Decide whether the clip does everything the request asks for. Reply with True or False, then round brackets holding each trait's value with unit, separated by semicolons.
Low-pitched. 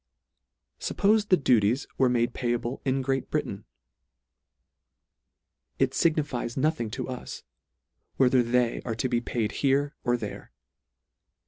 True (125 Hz)